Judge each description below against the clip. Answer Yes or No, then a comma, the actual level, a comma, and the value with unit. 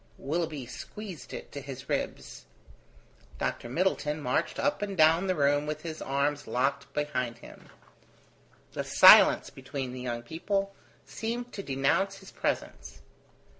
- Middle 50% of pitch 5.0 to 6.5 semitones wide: Yes, wide, 5.6 semitones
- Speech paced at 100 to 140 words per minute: Yes, slow, 135 wpm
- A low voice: No, medium, 150 Hz